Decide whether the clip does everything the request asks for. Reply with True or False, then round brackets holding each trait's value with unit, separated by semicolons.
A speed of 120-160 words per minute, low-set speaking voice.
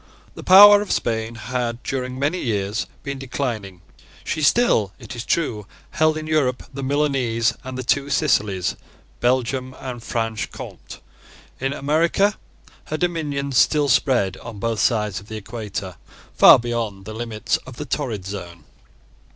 True (150 wpm; 125 Hz)